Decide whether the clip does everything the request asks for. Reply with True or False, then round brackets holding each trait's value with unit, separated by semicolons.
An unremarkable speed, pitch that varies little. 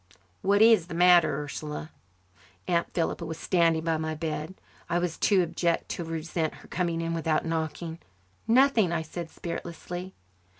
True (155 wpm; 1.7 semitones)